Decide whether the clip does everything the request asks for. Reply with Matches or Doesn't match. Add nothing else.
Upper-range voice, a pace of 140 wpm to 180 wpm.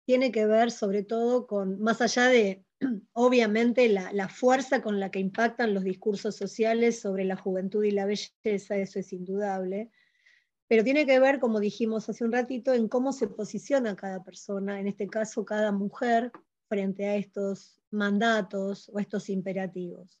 Matches